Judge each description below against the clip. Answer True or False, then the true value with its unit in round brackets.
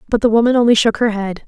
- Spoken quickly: True (285 wpm)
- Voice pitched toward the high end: True (225 Hz)